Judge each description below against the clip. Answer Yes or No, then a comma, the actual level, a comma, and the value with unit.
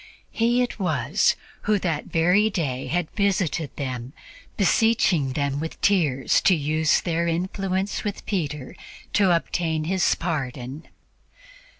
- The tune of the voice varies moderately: Yes, average, 4.9 semitones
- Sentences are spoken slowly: Yes, slow, 120 wpm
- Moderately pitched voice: Yes, medium, 165 Hz